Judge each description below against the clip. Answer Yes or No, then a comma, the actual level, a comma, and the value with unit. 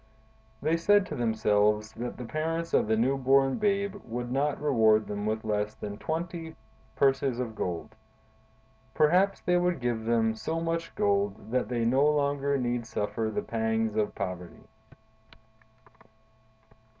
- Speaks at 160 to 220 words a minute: No, average, 145 wpm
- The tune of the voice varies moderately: No, wide, 5.8 semitones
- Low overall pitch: Yes, low, 120 Hz